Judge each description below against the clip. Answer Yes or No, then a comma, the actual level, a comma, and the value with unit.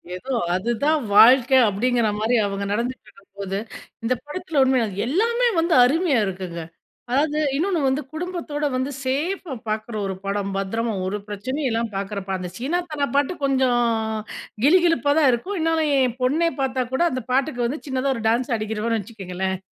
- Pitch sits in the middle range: No, very high, 255 Hz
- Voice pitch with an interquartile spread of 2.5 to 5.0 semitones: No, wide, 5.6 semitones